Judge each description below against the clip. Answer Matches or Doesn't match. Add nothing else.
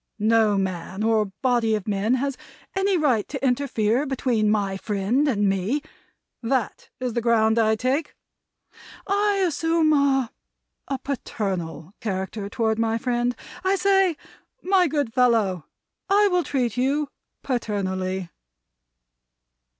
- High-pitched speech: Matches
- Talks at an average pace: Doesn't match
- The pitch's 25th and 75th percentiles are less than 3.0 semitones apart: Doesn't match